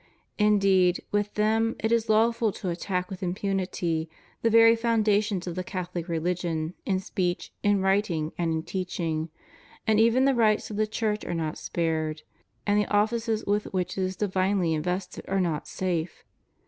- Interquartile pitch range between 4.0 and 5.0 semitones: No, average, 3.4 semitones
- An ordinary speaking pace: Yes, average, 165 wpm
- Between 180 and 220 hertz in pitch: Yes, high, 190 Hz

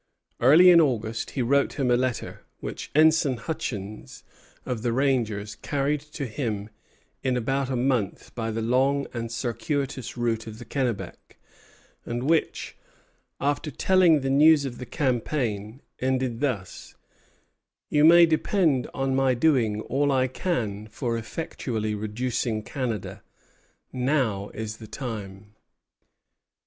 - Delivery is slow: Yes, slow, 130 wpm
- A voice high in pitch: No, low, 125 Hz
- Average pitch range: Yes, average, 4.0 semitones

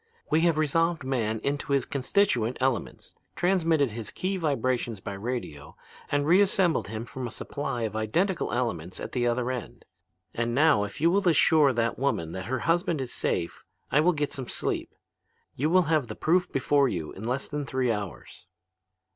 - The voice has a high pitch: No, low, 130 Hz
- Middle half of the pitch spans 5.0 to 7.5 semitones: Yes, wide, 5.5 semitones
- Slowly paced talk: No, average, 180 wpm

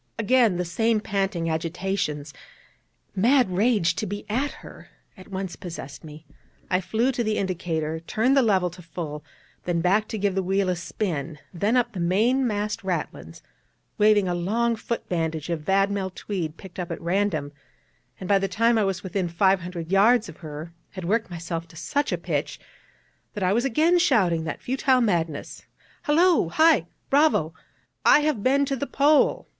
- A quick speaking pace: No, average, 175 wpm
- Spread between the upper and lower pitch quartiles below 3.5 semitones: No, average, 5.1 semitones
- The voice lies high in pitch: Yes, high, 195 Hz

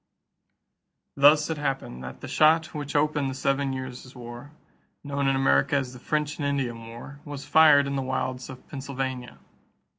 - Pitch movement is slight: Yes, narrow, 2.0 semitones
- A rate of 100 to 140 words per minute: No, average, 175 wpm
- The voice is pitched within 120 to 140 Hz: Yes, low, 135 Hz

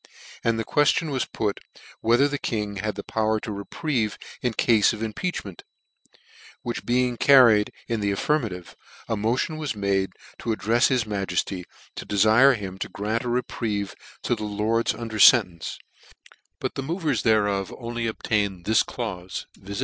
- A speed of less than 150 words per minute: No, average, 155 wpm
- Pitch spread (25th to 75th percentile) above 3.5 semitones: No, average, 3.1 semitones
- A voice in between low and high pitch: No, low, 110 Hz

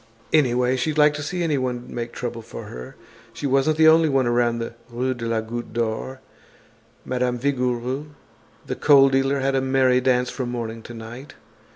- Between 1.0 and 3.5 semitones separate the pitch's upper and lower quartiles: Yes, narrow, 2.4 semitones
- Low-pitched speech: Yes, low, 125 Hz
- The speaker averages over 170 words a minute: Yes, average, 180 wpm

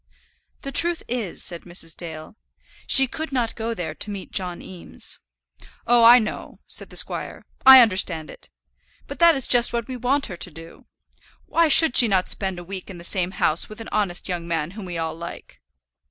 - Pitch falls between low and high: No, high, 195 Hz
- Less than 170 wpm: No, average, 200 wpm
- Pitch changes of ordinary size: No, wide, 5.8 semitones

